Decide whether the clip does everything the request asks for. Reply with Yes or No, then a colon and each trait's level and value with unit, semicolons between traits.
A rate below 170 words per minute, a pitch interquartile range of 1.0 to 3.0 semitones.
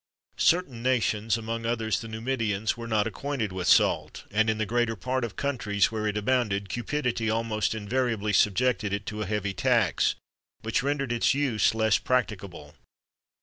No: average, 175 wpm; average, 2.7 semitones